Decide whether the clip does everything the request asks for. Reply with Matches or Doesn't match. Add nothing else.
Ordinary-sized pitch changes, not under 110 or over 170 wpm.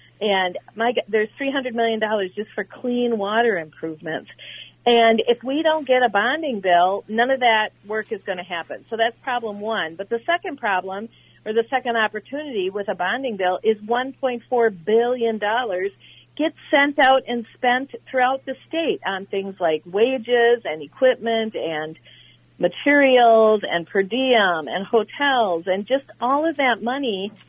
Matches